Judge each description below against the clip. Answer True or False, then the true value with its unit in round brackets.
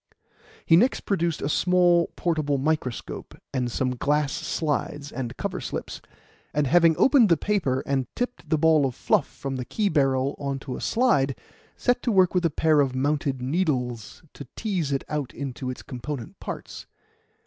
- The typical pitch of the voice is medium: True (145 Hz)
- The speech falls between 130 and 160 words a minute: False (170 wpm)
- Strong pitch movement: False (4.4 semitones)